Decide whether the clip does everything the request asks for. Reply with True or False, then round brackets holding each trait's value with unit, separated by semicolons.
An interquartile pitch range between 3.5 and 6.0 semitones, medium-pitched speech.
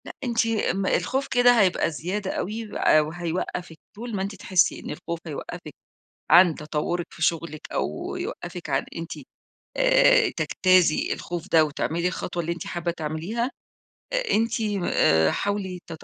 True (3.9 semitones; 175 Hz)